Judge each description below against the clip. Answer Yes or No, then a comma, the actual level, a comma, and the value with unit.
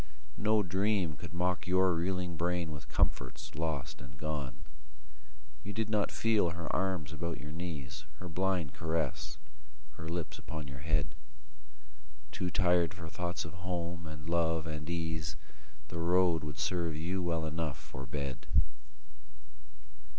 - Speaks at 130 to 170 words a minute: Yes, average, 145 wpm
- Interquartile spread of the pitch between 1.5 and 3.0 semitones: Yes, narrow, 2.6 semitones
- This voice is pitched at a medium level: No, very low, 85 Hz